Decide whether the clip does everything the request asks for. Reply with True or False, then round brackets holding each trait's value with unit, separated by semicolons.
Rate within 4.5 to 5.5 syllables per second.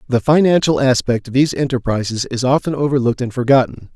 False (6.4 syllables/s)